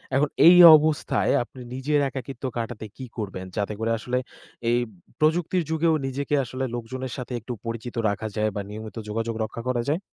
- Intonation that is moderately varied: Yes, average, 4.0 semitones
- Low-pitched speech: Yes, low, 125 Hz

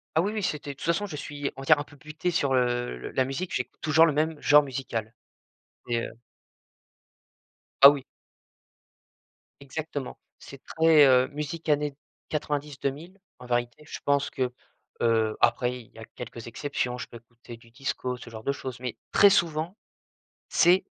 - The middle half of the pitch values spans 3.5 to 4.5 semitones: Yes, average, 3.8 semitones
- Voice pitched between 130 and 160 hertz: Yes, medium, 140 Hz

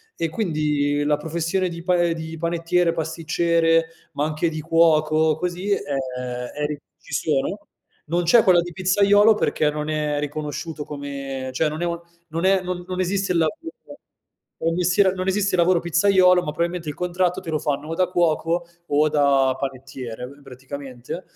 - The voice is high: No, medium, 165 Hz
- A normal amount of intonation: Yes, average, 3.2 semitones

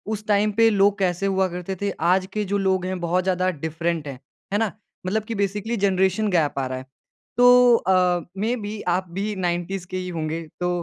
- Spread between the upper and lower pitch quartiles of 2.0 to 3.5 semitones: Yes, average, 2.8 semitones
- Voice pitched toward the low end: No, high, 190 Hz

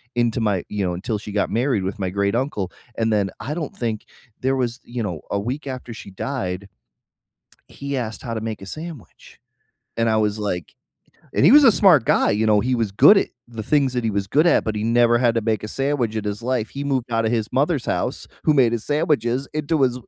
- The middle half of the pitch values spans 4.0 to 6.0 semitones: Yes, average, 4.3 semitones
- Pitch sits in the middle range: No, low, 115 Hz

